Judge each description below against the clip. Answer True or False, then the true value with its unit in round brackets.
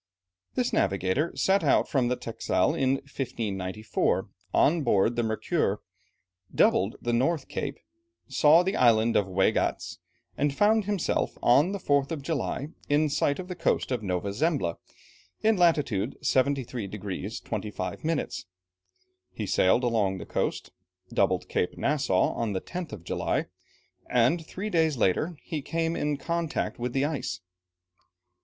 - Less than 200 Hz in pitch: True (135 Hz)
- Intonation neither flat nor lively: False (7.0 semitones)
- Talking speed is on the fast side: False (145 wpm)